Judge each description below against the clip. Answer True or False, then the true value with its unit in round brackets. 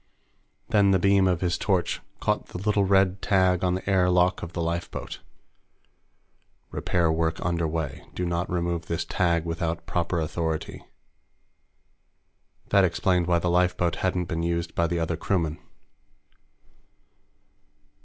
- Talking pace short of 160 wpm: True (140 wpm)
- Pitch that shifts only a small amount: True (1.7 semitones)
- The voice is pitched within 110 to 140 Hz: False (85 Hz)